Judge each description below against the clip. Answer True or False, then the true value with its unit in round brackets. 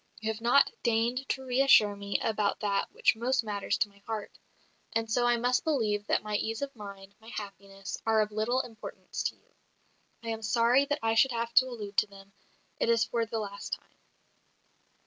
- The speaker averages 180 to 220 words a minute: True (200 wpm)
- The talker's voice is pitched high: True (225 Hz)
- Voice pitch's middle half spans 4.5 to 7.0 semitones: False (2.7 semitones)